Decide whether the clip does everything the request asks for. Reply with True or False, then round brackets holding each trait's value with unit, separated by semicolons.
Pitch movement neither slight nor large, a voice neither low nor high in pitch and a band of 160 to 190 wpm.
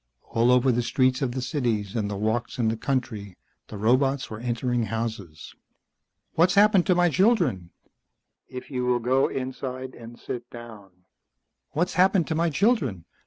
False (4.0 semitones; 125 Hz; 165 wpm)